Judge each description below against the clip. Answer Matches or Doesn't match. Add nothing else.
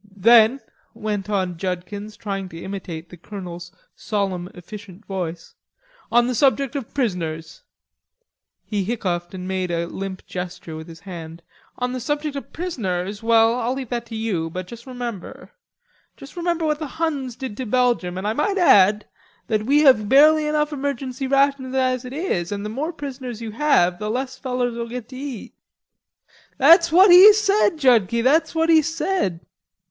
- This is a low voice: Doesn't match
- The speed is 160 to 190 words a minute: Matches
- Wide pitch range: Matches